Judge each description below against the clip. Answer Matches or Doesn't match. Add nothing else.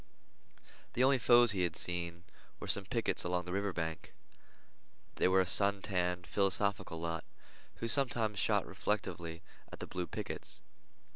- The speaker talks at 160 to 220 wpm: Doesn't match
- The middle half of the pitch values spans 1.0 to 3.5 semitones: Matches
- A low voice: Matches